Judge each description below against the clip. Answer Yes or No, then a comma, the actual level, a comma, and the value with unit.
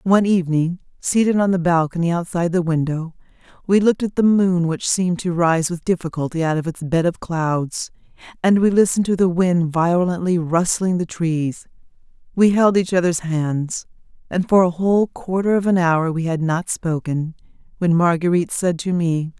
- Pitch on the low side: No, medium, 175 Hz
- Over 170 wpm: Yes, average, 180 wpm